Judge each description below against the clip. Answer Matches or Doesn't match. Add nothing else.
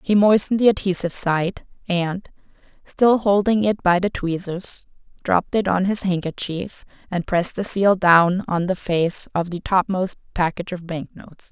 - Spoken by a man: Doesn't match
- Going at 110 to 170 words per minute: Matches